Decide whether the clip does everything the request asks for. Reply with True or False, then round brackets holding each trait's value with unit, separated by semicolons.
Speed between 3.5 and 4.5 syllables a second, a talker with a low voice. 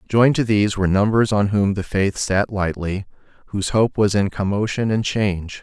False (5.4 syllables/s; 100 Hz)